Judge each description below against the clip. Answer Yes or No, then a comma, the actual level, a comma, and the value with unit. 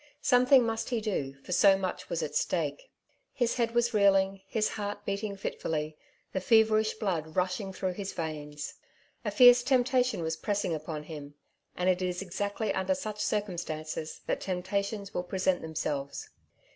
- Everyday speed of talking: Yes, average, 160 wpm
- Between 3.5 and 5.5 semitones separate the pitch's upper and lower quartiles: Yes, average, 4.4 semitones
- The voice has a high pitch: Yes, high, 195 Hz